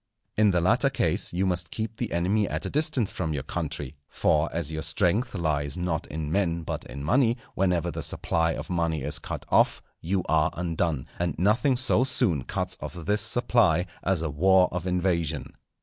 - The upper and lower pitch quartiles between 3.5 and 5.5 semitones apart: Yes, average, 4.1 semitones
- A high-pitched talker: No, very low, 90 Hz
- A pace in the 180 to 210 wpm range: Yes, average, 190 wpm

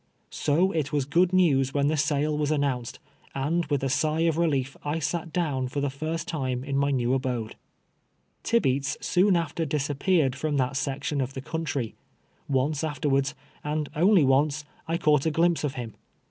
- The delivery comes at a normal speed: Yes, average, 180 wpm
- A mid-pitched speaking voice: Yes, medium, 145 Hz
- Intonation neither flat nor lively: Yes, average, 3.0 semitones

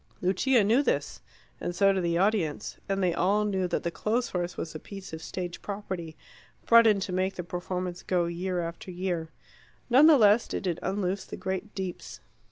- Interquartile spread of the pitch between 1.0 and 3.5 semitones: Yes, narrow, 2.6 semitones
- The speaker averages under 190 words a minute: No, average, 195 wpm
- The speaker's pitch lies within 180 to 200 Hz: Yes, medium, 185 Hz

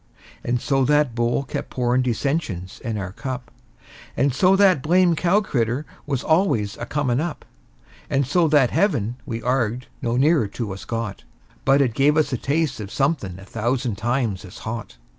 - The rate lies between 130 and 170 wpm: No, average, 180 wpm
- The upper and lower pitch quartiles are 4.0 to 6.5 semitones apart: Yes, average, 4.4 semitones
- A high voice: No, low, 125 Hz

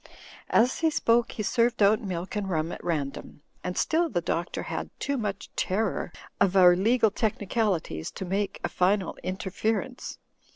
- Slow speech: No, average, 160 wpm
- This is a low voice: No, high, 200 Hz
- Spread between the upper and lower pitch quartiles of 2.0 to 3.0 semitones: No, average, 3.8 semitones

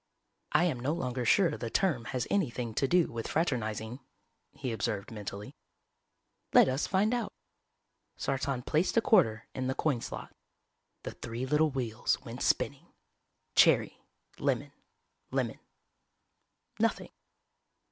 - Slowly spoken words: Yes, slow, 125 wpm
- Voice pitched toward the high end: No, low, 130 Hz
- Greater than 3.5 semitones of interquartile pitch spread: Yes, average, 5.3 semitones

